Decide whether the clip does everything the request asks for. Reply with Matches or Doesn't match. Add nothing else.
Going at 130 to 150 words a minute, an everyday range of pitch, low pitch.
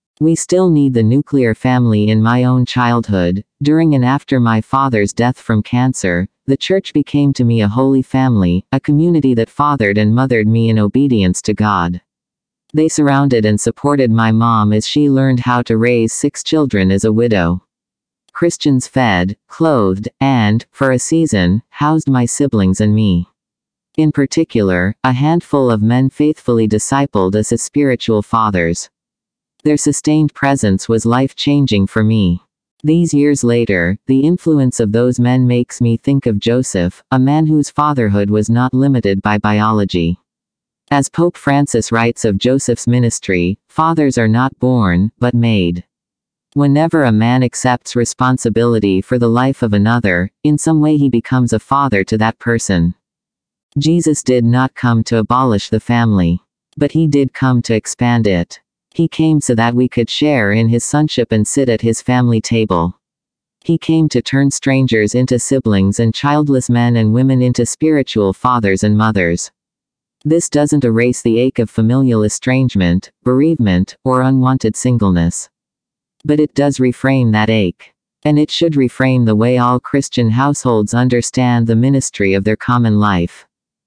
Doesn't match